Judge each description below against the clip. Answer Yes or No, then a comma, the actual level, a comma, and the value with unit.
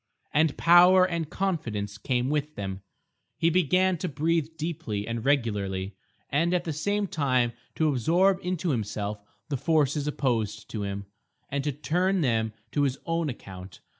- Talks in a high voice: No, medium, 145 Hz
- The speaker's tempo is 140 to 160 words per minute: Yes, average, 155 wpm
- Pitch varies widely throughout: Yes, wide, 7.0 semitones